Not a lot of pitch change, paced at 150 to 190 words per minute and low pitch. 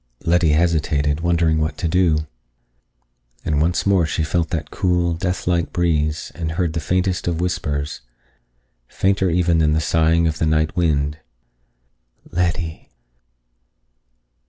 No: narrow, 2.1 semitones; slow, 135 wpm; very low, 80 Hz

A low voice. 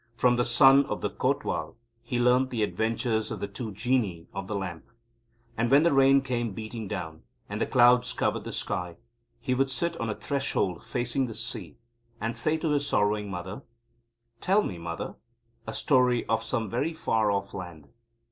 Yes: low, 115 Hz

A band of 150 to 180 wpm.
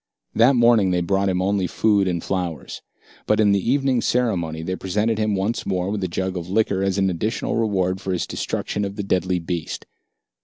No: average, 200 wpm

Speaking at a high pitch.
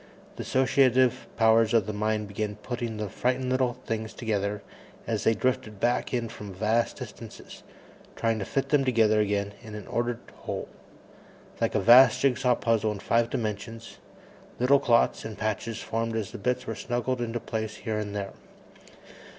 No: low, 115 Hz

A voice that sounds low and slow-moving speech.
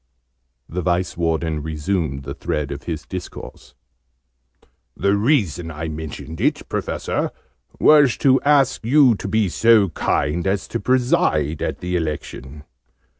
Yes: very low, 85 Hz; slow, 130 wpm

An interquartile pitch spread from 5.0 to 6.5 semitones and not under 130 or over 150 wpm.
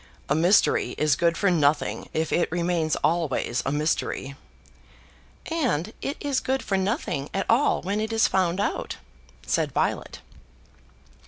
Yes: wide, 5.5 semitones; average, 145 wpm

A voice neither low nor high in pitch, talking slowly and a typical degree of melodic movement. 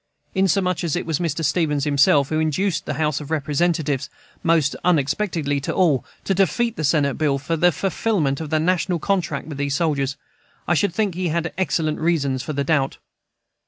No: medium, 155 Hz; average, 185 wpm; average, 3.6 semitones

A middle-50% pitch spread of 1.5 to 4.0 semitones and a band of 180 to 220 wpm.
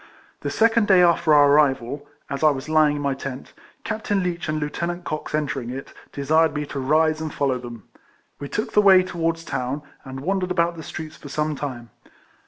Yes: average, 3.6 semitones; average, 200 wpm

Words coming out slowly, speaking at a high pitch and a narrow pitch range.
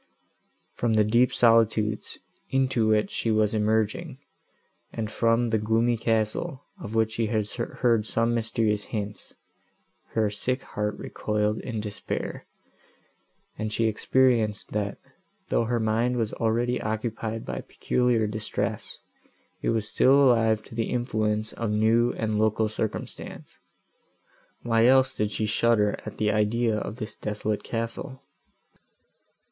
No: slow, 130 wpm; low, 110 Hz; narrow, 1.6 semitones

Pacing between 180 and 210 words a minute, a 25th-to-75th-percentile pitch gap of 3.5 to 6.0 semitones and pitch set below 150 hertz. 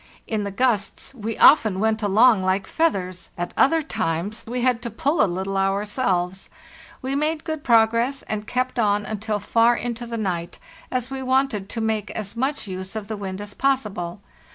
No: average, 185 wpm; average, 4.4 semitones; high, 220 Hz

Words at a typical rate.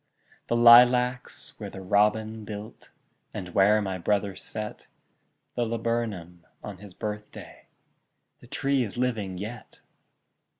No: slow, 120 wpm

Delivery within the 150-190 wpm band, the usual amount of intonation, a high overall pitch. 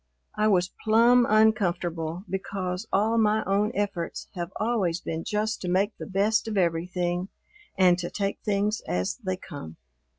Yes: average, 155 wpm; average, 3.3 semitones; high, 195 Hz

